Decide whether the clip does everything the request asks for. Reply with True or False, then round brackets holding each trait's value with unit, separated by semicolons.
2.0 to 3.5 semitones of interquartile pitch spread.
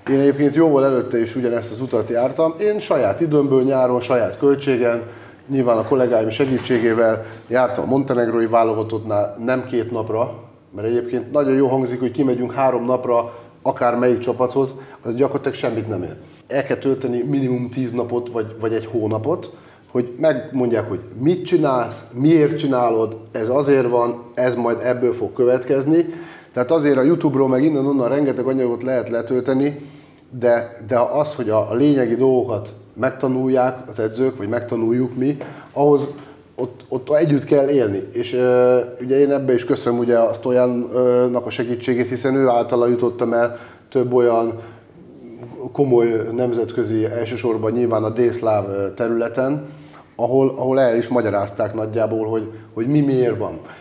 True (2.4 semitones)